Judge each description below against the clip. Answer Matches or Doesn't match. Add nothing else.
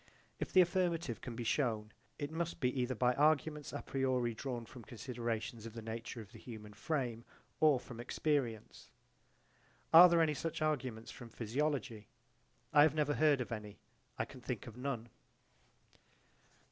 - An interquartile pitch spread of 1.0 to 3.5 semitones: Doesn't match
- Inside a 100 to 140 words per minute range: Doesn't match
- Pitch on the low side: Matches